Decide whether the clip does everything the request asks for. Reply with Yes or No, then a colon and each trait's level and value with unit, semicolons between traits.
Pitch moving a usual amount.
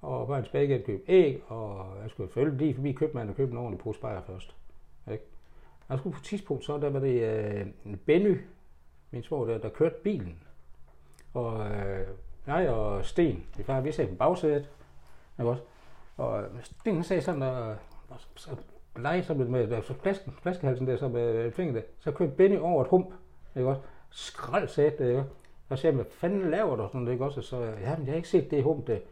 No: wide, 6.7 semitones